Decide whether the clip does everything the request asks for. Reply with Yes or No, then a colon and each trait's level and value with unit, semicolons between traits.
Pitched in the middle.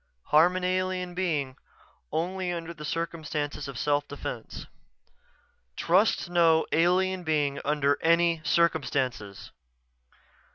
Yes: medium, 165 Hz